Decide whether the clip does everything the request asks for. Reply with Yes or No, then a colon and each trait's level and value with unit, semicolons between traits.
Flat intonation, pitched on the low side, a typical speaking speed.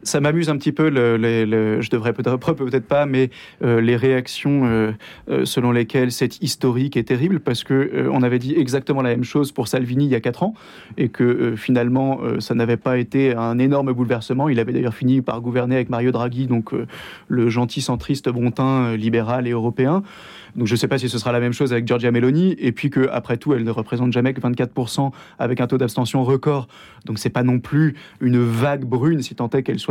No: narrow, 2.3 semitones; low, 125 Hz; fast, 230 wpm